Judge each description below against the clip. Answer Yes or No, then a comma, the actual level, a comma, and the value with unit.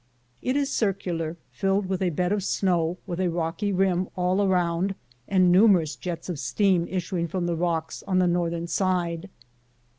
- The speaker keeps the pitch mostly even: Yes, narrow, 2.2 semitones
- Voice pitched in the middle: Yes, medium, 180 Hz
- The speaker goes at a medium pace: Yes, average, 170 wpm